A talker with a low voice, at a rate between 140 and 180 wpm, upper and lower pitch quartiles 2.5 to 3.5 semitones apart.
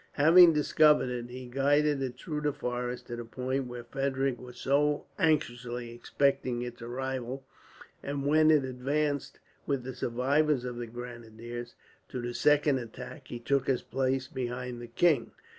Yes: low, 130 Hz; average, 160 wpm; average, 2.8 semitones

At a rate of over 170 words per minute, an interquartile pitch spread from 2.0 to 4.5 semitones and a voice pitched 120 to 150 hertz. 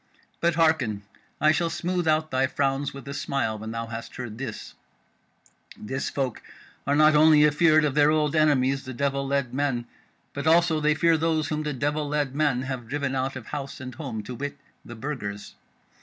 Yes: average, 190 wpm; average, 2.8 semitones; medium, 140 Hz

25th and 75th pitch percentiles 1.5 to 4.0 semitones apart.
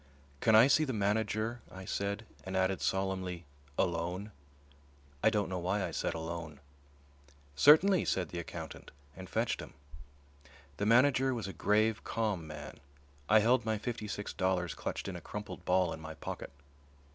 Yes: average, 3.6 semitones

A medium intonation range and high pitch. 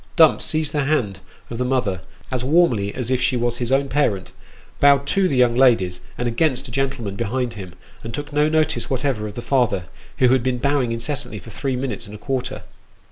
No: average, 3.1 semitones; low, 125 Hz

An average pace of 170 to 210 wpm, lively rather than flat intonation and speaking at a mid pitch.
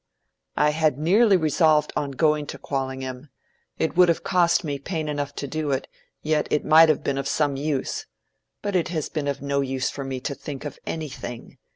No: average, 200 wpm; narrow, 2.4 semitones; medium, 150 Hz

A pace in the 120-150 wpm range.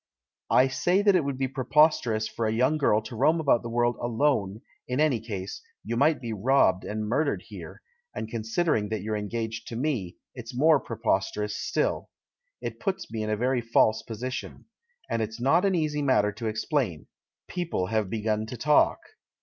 No: average, 190 wpm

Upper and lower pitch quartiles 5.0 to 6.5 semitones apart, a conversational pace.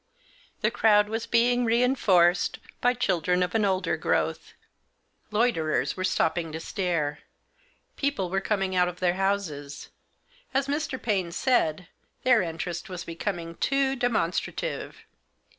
No: wide, 5.5 semitones; slow, 130 wpm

